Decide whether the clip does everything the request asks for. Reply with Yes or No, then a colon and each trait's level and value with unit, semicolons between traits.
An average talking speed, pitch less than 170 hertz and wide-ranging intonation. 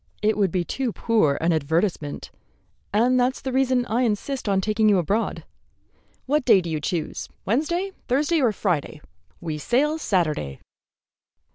No: average, 150 wpm; high, 215 Hz; wide, 7.0 semitones